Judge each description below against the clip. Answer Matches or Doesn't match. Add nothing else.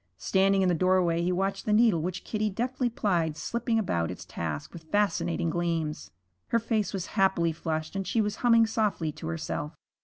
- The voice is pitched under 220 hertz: Matches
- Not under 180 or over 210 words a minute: Matches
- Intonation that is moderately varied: Matches